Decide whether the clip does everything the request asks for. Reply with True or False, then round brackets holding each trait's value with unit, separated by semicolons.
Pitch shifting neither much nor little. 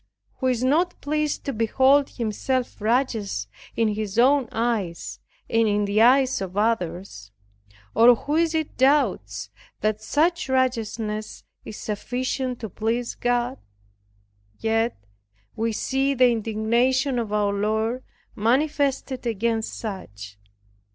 True (3.6 semitones)